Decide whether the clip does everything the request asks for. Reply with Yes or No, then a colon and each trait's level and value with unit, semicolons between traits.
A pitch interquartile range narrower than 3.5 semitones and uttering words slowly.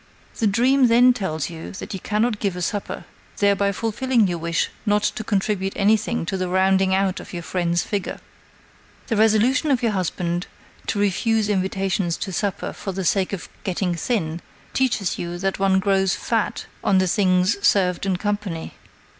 No: average, 2.7 semitones; average, 170 wpm